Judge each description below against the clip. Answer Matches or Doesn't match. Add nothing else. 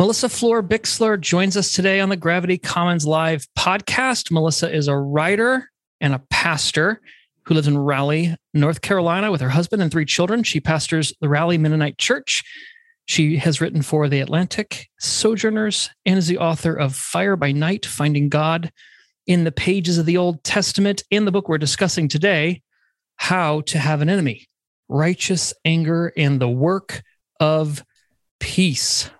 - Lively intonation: Doesn't match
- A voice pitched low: Doesn't match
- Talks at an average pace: Matches